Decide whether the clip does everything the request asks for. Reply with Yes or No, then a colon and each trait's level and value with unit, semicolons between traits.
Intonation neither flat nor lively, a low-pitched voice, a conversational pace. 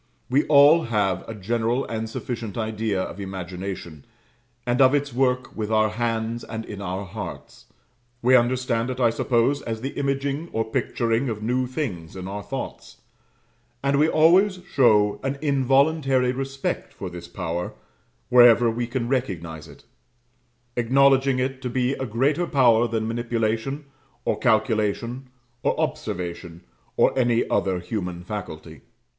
Yes: average, 4.2 semitones; low, 120 Hz; average, 145 wpm